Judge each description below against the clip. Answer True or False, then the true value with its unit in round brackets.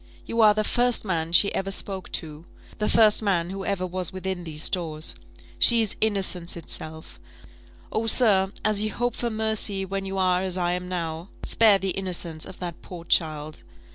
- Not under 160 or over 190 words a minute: True (185 wpm)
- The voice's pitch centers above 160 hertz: True (190 Hz)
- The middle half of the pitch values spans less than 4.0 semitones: True (3.5 semitones)